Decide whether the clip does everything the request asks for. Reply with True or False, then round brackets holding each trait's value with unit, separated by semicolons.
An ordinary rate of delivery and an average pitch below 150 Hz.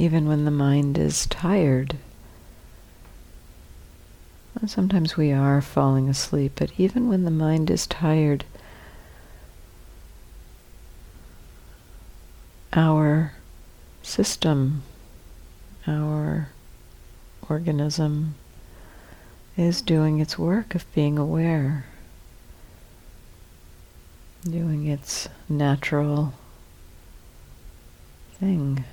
False (70 wpm; 140 Hz)